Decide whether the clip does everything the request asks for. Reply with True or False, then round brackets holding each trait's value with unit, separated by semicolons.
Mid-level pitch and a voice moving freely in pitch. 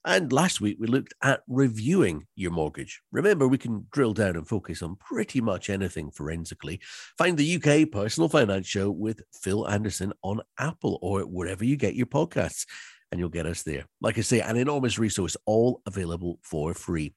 False (105 Hz; 5.7 semitones)